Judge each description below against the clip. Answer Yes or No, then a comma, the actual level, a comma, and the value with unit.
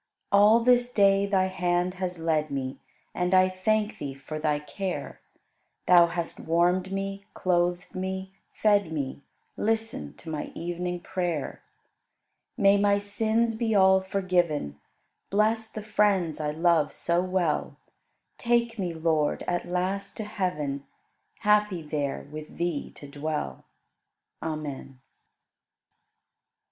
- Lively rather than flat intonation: No, average, 4.0 semitones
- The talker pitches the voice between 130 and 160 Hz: No, medium, 180 Hz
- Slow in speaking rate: Yes, slow, 125 wpm